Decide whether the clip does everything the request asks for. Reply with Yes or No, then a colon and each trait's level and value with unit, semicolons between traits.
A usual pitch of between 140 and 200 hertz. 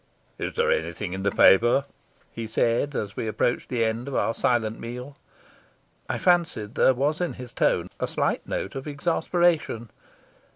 No: low, 120 Hz